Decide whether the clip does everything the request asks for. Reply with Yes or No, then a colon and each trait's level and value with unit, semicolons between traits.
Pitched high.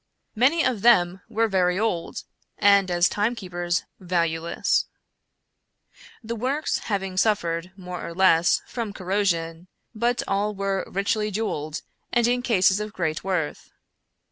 Yes: high, 195 Hz